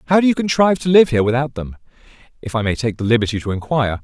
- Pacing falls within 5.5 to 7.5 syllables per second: No, 7.8 syllables/s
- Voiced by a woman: No, male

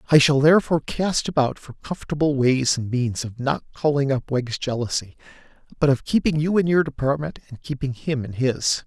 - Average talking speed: Yes, average, 190 wpm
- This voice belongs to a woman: No, male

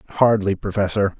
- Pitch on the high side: No, low, 100 Hz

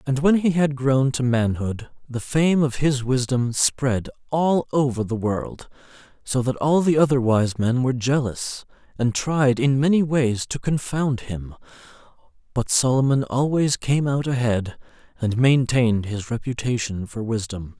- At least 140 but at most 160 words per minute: Yes, average, 155 wpm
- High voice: No, low, 130 Hz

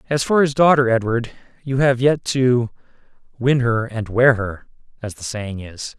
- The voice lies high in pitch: No, low, 125 Hz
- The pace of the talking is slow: No, average, 180 wpm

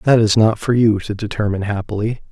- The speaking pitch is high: No, low, 110 Hz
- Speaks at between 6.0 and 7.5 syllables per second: Yes, 6.1 syllables/s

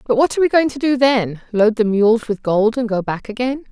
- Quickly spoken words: Yes, fast, 260 wpm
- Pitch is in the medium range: No, high, 235 Hz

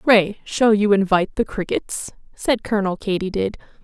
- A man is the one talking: No, female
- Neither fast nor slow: Yes, average, 155 wpm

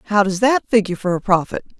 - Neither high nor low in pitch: No, high, 200 Hz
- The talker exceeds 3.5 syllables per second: Yes, 6.8 syllables/s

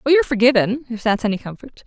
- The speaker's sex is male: No, female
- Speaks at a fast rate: No, average, 195 wpm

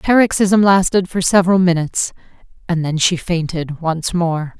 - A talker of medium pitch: Yes, medium, 175 Hz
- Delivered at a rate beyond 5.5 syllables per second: No, 5.0 syllables/s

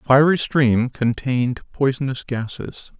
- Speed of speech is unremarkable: No, slow, 100 wpm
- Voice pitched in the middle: No, low, 130 Hz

